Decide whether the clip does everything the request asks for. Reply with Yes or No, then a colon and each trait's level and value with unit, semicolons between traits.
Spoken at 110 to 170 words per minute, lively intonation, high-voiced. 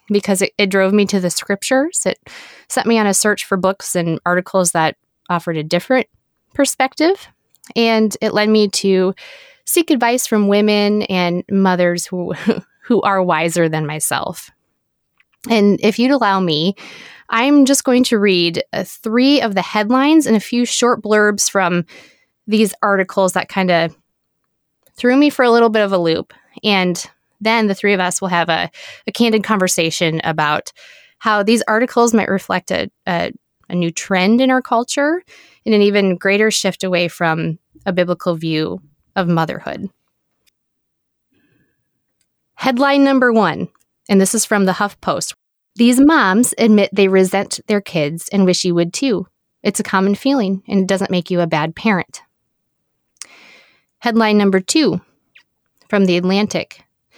No: average, 160 wpm; average, 4.2 semitones; high, 200 Hz